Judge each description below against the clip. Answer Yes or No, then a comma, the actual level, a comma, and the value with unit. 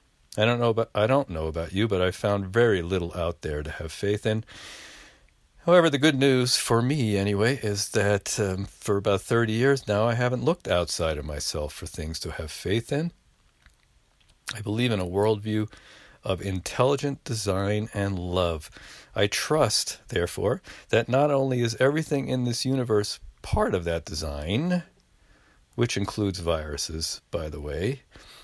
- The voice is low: Yes, low, 105 Hz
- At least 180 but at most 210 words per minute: No, average, 165 wpm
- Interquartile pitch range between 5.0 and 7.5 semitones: Yes, wide, 5.4 semitones